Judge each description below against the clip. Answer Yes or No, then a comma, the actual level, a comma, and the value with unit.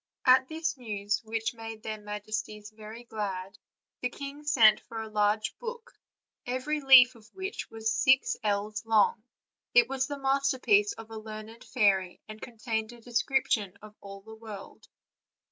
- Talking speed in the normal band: Yes, average, 155 wpm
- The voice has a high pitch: Yes, high, 220 Hz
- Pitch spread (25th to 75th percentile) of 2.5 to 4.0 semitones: Yes, average, 3.4 semitones